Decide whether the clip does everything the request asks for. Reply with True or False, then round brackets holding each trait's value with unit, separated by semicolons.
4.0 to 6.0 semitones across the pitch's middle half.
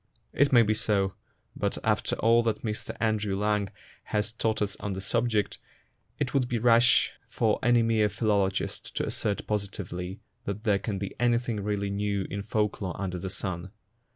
False (2.5 semitones)